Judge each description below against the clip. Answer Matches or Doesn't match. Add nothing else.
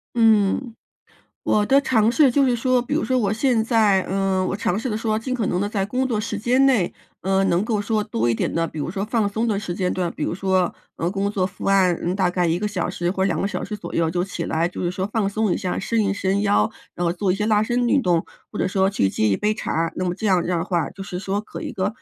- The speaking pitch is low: Doesn't match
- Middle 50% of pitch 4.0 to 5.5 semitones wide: Doesn't match